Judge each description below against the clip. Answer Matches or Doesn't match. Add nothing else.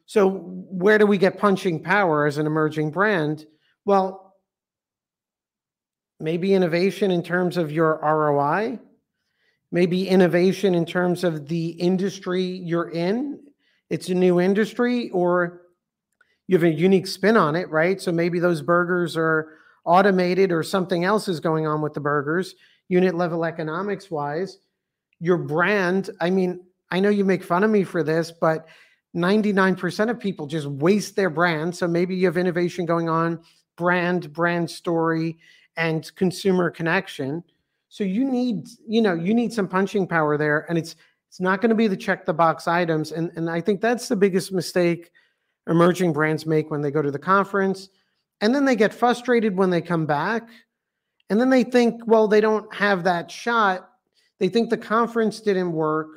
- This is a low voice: Doesn't match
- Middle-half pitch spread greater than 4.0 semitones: Doesn't match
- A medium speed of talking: Matches